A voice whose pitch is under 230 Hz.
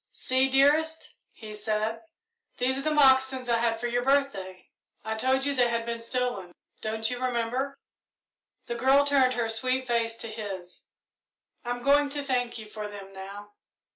No: high, 245 Hz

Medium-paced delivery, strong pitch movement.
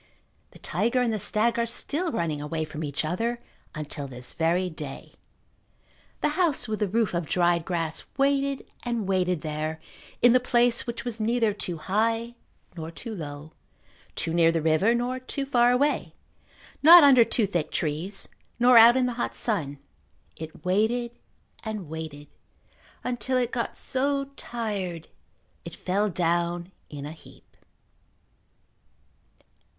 Yes: average, 145 wpm; wide, 6.7 semitones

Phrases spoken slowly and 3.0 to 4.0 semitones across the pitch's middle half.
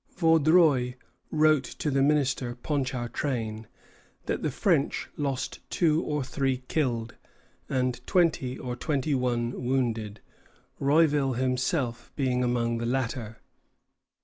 Yes: slow, 110 wpm; average, 3.3 semitones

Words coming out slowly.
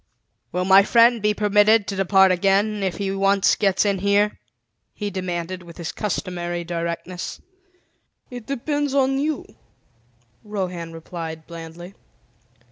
Yes: slow, 125 wpm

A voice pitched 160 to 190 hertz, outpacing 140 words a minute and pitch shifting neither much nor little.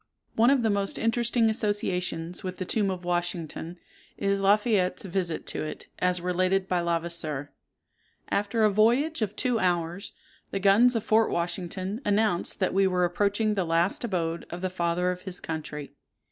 Yes: medium, 185 Hz; average, 170 wpm; average, 3.3 semitones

